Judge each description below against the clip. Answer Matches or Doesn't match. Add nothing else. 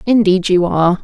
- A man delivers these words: Doesn't match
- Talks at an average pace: Matches